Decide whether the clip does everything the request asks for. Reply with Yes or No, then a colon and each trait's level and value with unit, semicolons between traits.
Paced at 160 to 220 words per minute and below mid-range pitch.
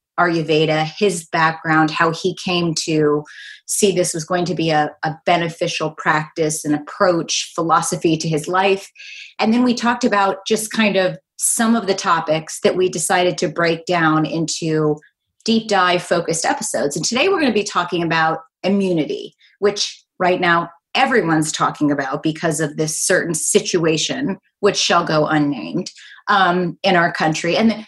No: average, 165 wpm; medium, 175 Hz